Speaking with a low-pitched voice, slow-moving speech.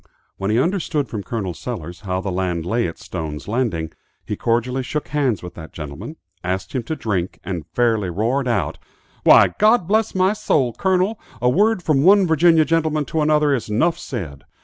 No: low, 125 Hz; average, 185 wpm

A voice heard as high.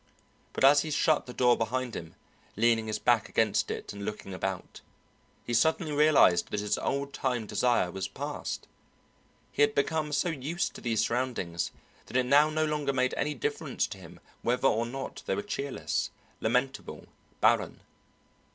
No: low, 125 Hz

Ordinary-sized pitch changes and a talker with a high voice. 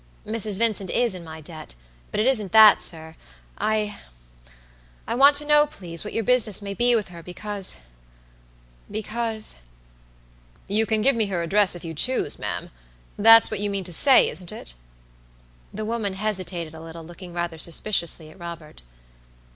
Yes: average, 4.6 semitones; high, 195 Hz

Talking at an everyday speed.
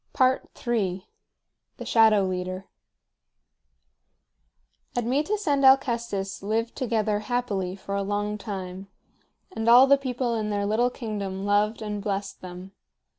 No: slow, 120 wpm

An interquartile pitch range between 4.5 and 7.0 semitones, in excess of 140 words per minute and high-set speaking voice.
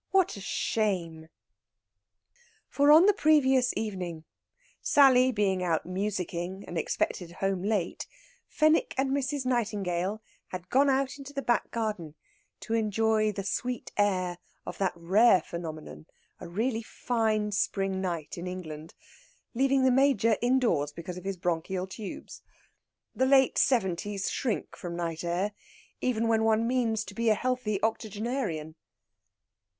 No: wide, 5.6 semitones; slow, 135 wpm; high, 210 Hz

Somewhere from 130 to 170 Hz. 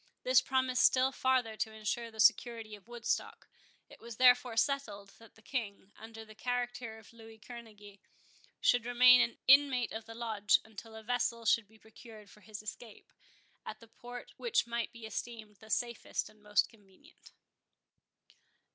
No: high, 230 Hz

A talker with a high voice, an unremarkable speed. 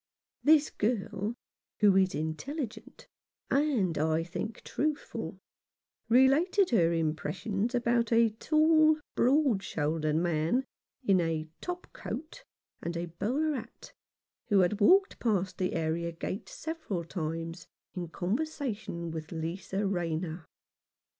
No: high, 195 Hz; slow, 110 wpm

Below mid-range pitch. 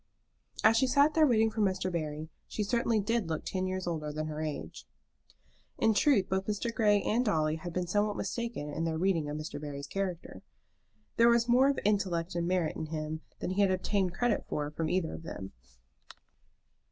No: medium, 185 Hz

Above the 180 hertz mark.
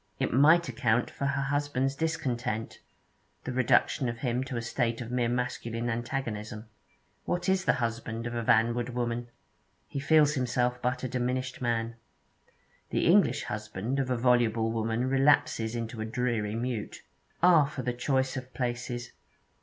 No: low, 125 Hz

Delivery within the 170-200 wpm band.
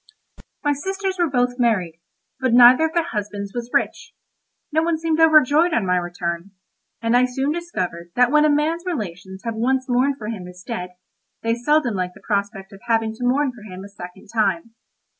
Yes: average, 195 wpm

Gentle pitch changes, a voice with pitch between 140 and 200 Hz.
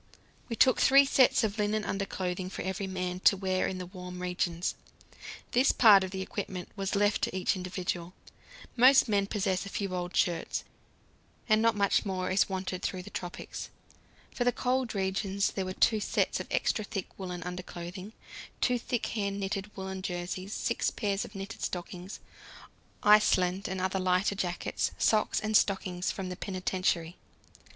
Yes: narrow, 2.2 semitones; high, 190 Hz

